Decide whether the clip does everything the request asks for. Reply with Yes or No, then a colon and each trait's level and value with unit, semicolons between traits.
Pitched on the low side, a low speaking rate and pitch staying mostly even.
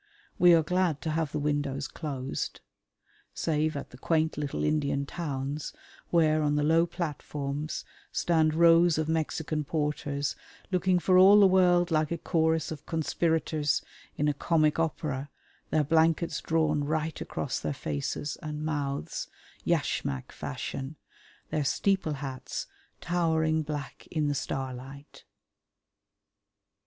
No: medium, 155 Hz; slow, 130 wpm; narrow, 2.2 semitones